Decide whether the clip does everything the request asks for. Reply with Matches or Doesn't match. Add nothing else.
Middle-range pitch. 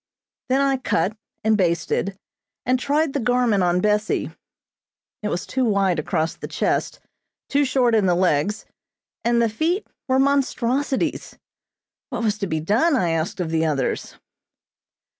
Doesn't match